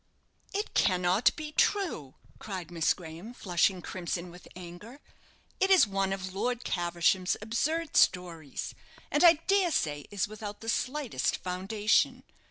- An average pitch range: No, wide, 5.8 semitones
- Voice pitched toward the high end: Yes, high, 195 Hz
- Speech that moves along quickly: No, slow, 135 wpm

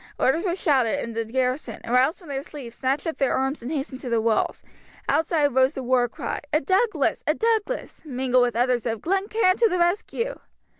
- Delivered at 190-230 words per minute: Yes, fast, 205 wpm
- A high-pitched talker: Yes, very high, 270 Hz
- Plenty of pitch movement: Yes, wide, 5.7 semitones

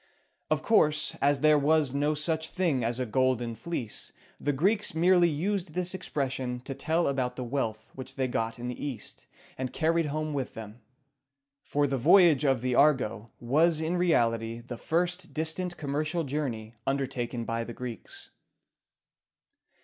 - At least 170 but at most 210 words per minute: No, average, 155 wpm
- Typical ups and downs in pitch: Yes, average, 4.4 semitones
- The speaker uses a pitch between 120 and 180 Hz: Yes, medium, 140 Hz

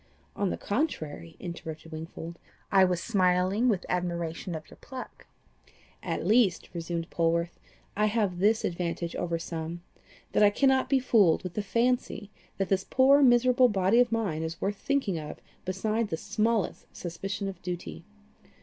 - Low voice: No, high, 190 Hz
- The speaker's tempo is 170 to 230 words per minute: No, average, 155 wpm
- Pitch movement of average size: Yes, average, 4.8 semitones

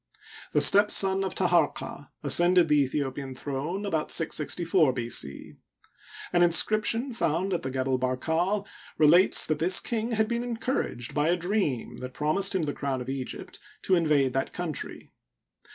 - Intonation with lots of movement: Yes, wide, 5.8 semitones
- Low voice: No, medium, 165 Hz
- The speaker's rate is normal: Yes, average, 170 wpm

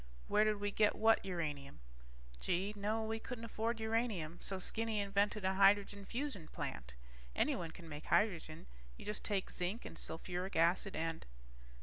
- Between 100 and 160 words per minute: Yes, average, 155 wpm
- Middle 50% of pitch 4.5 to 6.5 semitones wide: No, average, 4.0 semitones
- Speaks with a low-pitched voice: No, high, 200 Hz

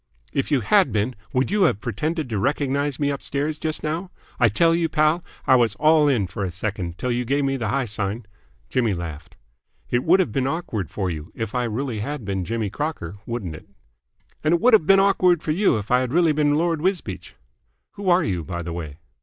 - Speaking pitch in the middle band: No, low, 130 Hz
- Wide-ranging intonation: Yes, wide, 7.0 semitones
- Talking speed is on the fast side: Yes, fast, 220 wpm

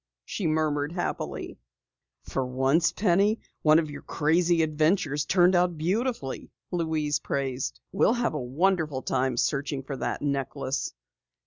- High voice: No, medium, 155 Hz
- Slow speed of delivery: Yes, slow, 130 wpm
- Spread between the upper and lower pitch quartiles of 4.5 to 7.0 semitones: No, average, 4.1 semitones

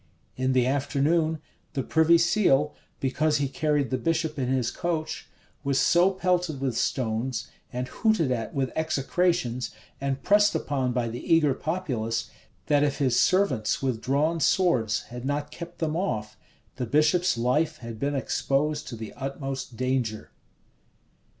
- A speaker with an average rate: Yes, average, 150 wpm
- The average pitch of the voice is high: No, medium, 140 Hz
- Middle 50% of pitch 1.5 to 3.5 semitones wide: No, average, 4.0 semitones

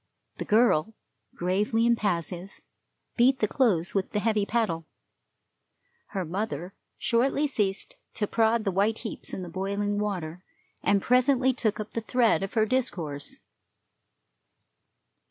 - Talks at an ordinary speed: No, slow, 130 wpm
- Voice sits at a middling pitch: No, high, 210 Hz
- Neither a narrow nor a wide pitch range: Yes, average, 3.7 semitones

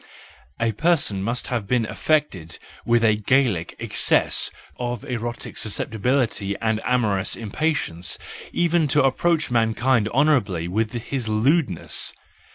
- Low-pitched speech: Yes, low, 115 Hz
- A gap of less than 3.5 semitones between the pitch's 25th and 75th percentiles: No, average, 4.1 semitones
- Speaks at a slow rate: Yes, slow, 120 wpm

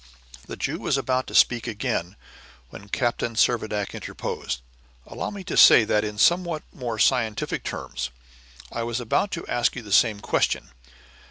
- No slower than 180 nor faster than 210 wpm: No, average, 160 wpm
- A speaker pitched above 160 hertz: No, low, 115 Hz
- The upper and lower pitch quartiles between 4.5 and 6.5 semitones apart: No, average, 3.2 semitones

